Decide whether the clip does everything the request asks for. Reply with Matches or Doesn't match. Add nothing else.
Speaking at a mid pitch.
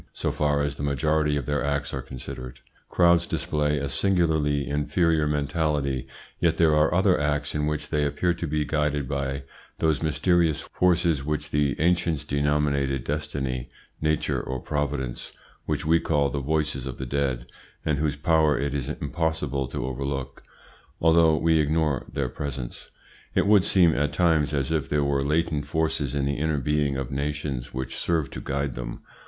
Doesn't match